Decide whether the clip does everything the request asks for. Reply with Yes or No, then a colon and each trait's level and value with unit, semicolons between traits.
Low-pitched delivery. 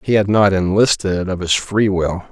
Yes: very low, 95 Hz